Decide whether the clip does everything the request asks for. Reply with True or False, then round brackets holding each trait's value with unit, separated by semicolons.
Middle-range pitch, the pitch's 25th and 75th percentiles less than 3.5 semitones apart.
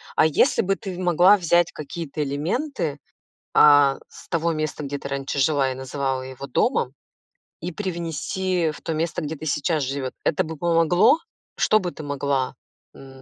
False (155 Hz; 3.8 semitones)